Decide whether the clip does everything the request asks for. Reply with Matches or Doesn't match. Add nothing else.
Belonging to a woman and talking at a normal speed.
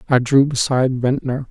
Doesn't match